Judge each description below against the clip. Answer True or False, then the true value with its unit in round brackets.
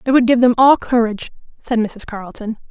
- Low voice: False (235 Hz)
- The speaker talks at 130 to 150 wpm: False (200 wpm)